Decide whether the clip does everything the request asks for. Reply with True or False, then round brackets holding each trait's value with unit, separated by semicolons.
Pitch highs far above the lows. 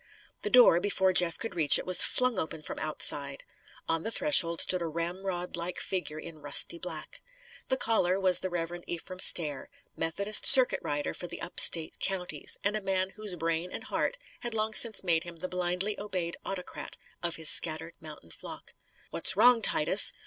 False (3.3 semitones)